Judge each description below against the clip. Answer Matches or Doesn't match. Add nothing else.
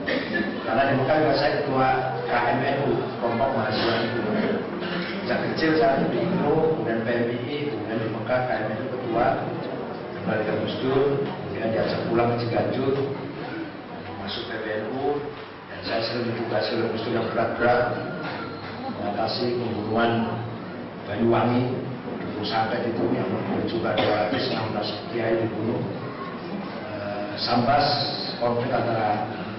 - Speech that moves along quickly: Doesn't match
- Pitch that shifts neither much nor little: Matches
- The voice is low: Matches